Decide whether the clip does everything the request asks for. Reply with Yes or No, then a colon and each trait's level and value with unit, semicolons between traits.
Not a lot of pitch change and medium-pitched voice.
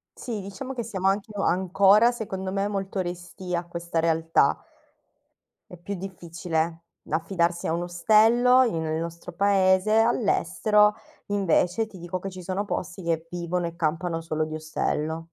No: average, 3.0 semitones; medium, 180 Hz